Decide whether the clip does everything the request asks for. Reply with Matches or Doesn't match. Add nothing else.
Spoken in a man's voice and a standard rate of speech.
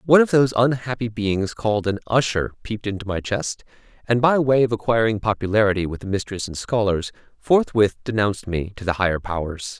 Matches